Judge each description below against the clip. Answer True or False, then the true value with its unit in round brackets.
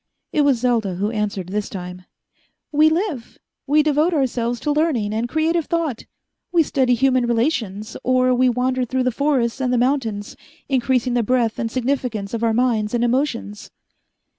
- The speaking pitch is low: False (250 Hz)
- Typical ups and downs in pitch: True (3.6 semitones)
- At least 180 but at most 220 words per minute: False (165 wpm)